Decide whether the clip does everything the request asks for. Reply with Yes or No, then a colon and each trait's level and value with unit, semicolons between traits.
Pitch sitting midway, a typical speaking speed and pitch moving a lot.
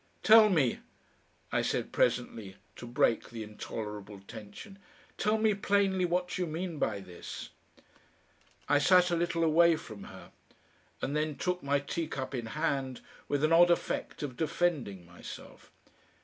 Yes: medium, 150 Hz; average, 145 wpm; wide, 7.2 semitones